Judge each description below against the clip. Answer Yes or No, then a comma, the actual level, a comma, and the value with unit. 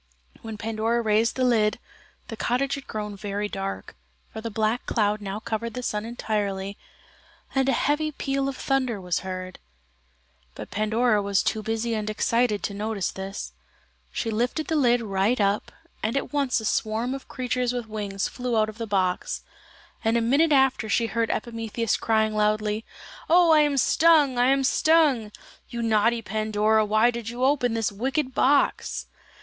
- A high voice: Yes, high, 225 Hz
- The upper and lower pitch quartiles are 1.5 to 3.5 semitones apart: Yes, average, 3.0 semitones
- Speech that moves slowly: No, average, 170 wpm